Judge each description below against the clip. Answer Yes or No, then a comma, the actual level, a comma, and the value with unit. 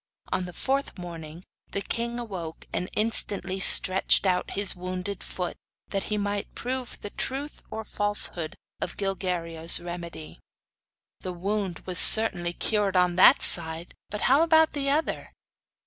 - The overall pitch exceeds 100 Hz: Yes, high, 190 Hz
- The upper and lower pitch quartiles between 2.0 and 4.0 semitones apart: Yes, average, 3.7 semitones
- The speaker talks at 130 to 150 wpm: Yes, average, 145 wpm